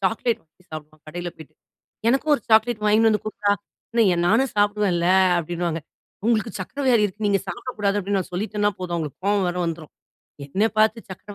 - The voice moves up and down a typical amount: Yes, average, 3.8 semitones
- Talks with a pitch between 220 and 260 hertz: No, high, 205 Hz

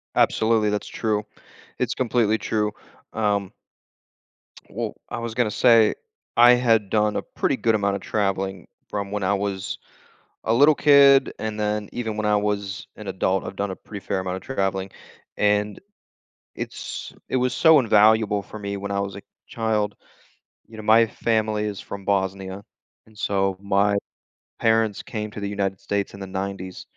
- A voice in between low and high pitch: No, low, 105 Hz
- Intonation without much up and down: Yes, narrow, 1.9 semitones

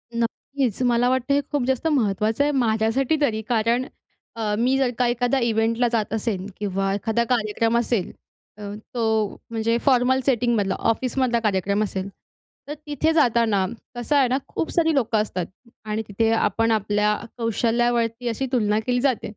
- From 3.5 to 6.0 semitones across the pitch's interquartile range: No, average, 2.8 semitones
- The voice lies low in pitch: No, high, 230 Hz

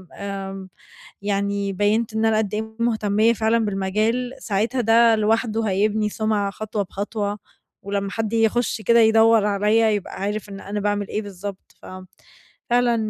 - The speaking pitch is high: Yes, high, 215 Hz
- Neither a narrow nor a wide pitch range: No, narrow, 1.8 semitones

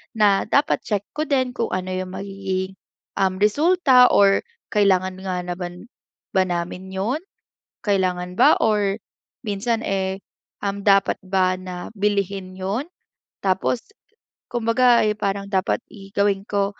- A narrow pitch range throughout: Yes, narrow, 2.1 semitones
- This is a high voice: Yes, high, 195 Hz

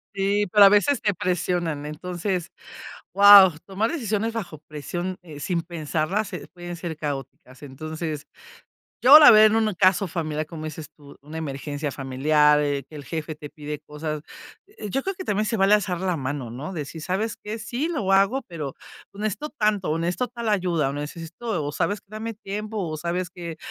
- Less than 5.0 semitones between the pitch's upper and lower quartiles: No, average, 5.3 semitones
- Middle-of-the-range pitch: Yes, medium, 175 Hz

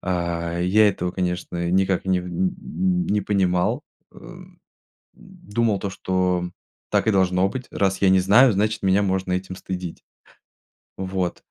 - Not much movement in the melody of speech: Yes, narrow, 1.8 semitones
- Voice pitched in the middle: No, very low, 95 Hz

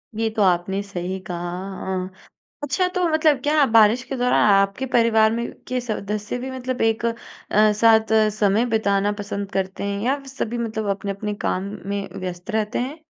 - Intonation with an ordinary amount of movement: Yes, average, 3.8 semitones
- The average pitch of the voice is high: Yes, high, 220 Hz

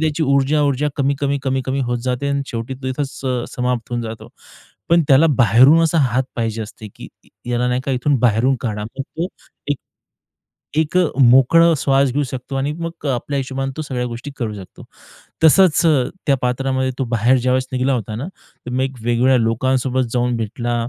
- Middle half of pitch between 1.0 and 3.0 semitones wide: Yes, narrow, 2.5 semitones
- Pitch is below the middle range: Yes, low, 130 Hz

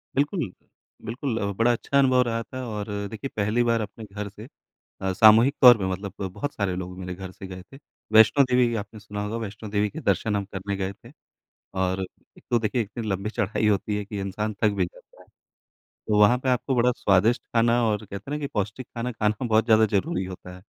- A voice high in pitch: No, low, 105 Hz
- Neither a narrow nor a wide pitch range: Yes, average, 3.1 semitones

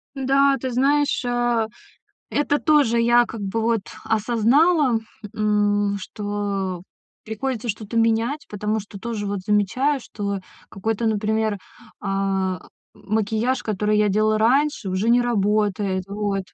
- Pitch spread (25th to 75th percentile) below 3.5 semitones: Yes, average, 2.9 semitones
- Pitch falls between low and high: No, high, 215 Hz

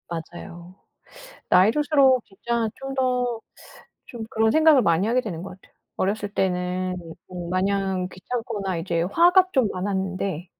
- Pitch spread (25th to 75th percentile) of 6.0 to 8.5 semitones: No, average, 5.3 semitones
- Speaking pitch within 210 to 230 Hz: No, high, 195 Hz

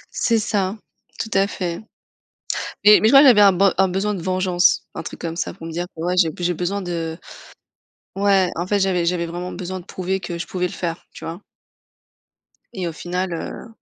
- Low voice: No, medium, 180 Hz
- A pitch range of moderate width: No, narrow, 2.2 semitones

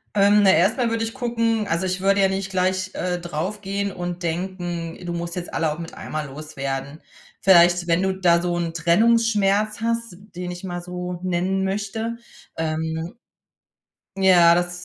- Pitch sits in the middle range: Yes, medium, 180 Hz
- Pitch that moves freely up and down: No, average, 2.7 semitones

